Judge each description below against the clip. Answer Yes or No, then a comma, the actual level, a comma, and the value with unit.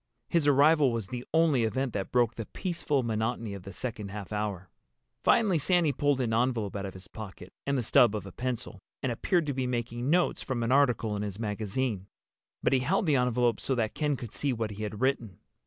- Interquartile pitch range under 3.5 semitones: No, average, 4.4 semitones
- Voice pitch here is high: No, low, 120 Hz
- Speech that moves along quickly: Yes, fast, 220 wpm